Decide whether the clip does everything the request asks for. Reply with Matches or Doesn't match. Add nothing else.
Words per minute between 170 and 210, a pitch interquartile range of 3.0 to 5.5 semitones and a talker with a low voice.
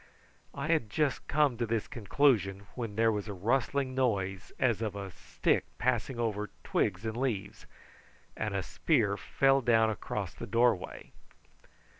Doesn't match